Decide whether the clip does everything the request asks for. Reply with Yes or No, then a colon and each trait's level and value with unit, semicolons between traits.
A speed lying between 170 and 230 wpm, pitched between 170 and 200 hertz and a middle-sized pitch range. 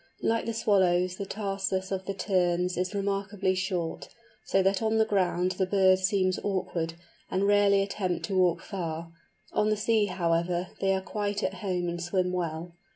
No: average, 175 wpm; high, 190 Hz; narrow, 2.0 semitones